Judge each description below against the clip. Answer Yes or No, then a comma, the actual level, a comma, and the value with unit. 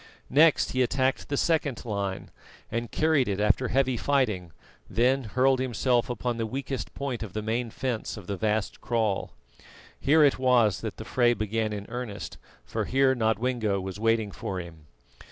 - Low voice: Yes, low, 120 Hz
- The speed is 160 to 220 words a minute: Yes, average, 170 wpm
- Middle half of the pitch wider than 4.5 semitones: No, average, 3.6 semitones